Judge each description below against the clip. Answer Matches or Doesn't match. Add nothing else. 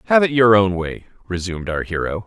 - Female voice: Doesn't match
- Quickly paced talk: Matches